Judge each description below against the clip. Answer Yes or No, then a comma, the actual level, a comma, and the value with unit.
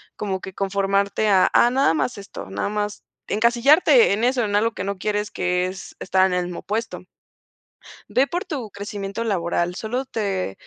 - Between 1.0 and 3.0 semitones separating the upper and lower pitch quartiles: No, average, 3.4 semitones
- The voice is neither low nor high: No, high, 205 Hz